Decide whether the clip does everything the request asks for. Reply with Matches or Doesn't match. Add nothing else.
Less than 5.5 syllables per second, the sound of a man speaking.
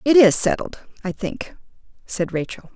Doesn't match